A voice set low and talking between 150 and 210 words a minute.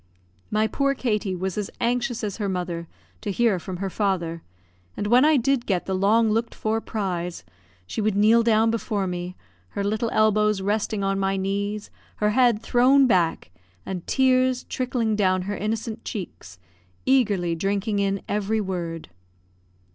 No: high, 210 Hz; average, 160 wpm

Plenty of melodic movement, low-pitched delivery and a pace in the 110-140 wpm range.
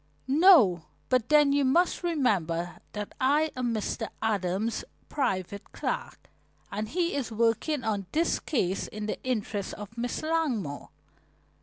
No: wide, 6.0 semitones; high, 230 Hz; slow, 135 wpm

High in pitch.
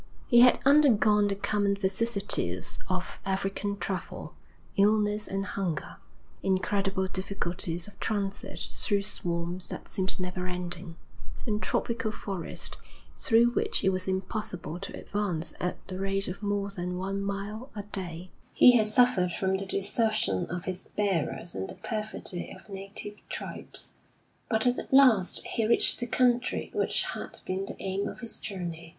Yes: high, 195 Hz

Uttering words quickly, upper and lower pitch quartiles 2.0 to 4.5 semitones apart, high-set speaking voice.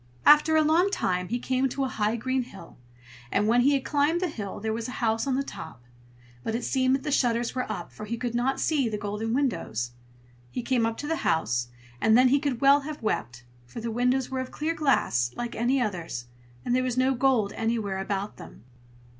Yes: fast, 225 wpm; average, 4.1 semitones; high, 245 Hz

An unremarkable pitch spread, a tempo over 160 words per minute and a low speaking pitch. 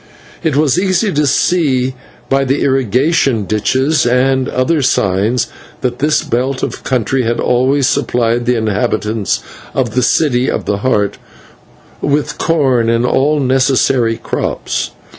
No: average, 3.0 semitones; slow, 135 wpm; low, 130 Hz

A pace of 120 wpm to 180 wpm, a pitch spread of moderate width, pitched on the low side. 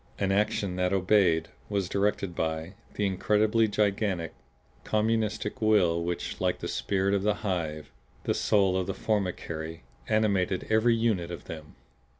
Yes: average, 145 wpm; average, 3.3 semitones; low, 100 Hz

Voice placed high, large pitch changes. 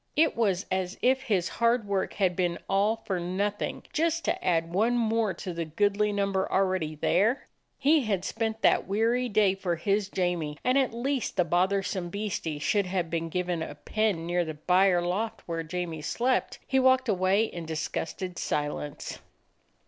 No: high, 195 Hz; average, 4.1 semitones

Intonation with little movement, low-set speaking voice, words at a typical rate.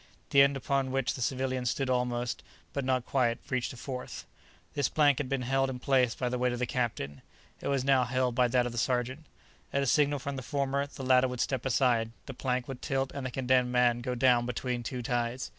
No: narrow, 1.6 semitones; low, 130 Hz; fast, 230 wpm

